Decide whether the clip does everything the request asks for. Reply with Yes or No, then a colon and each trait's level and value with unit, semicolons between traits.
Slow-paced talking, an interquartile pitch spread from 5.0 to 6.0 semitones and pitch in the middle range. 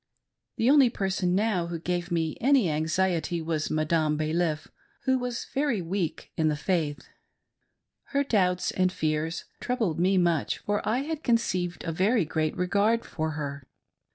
No: average, 155 wpm; wide, 5.4 semitones; medium, 175 Hz